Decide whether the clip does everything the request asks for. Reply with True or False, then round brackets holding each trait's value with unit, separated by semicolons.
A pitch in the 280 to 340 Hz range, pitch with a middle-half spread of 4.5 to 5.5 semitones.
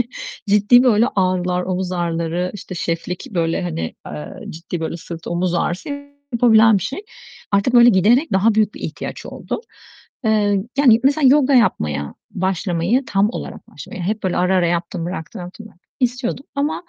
False (190 Hz; 5.2 semitones)